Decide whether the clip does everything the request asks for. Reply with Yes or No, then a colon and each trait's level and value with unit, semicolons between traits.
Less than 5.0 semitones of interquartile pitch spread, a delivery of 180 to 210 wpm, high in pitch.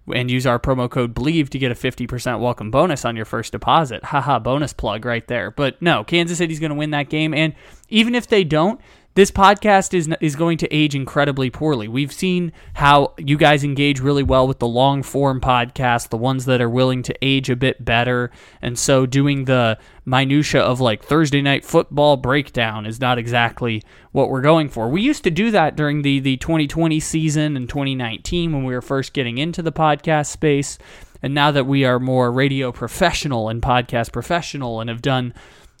No: average, 3.7 semitones; average, 200 wpm; medium, 140 Hz